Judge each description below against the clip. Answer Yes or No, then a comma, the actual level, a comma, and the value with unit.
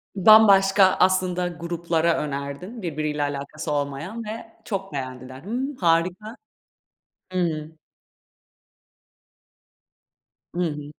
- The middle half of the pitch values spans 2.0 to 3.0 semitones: No, average, 4.7 semitones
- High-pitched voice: No, medium, 170 Hz